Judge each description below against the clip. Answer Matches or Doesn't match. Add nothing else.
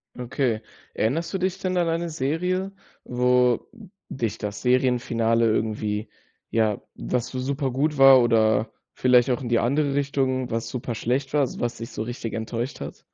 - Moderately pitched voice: Doesn't match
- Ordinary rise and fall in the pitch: Matches